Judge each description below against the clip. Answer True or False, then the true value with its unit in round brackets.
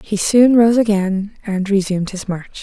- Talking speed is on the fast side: False (185 wpm)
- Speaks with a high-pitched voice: True (205 Hz)